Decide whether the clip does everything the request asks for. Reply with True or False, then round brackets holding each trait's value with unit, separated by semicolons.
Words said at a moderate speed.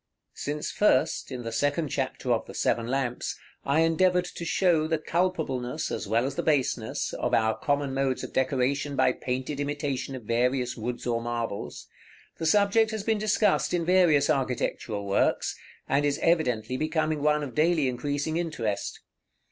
True (170 wpm)